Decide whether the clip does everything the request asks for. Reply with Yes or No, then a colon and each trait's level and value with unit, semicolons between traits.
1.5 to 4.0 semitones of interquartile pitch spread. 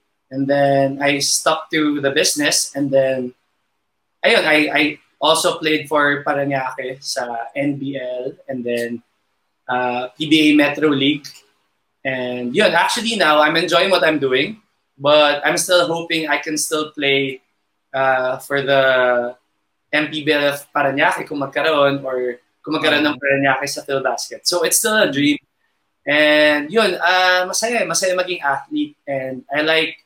Yes: average, 3.0 semitones